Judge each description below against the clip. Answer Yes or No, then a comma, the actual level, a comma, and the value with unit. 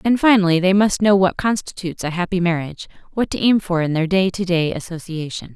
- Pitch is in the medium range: Yes, medium, 180 Hz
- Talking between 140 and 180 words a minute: No, fast, 205 wpm